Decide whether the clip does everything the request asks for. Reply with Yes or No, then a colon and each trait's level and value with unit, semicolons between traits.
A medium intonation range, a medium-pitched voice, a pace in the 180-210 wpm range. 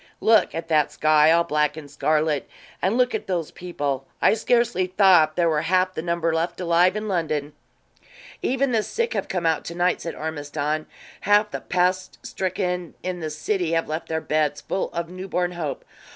Yes: average, 3.0 semitones; medium, 170 Hz; average, 185 wpm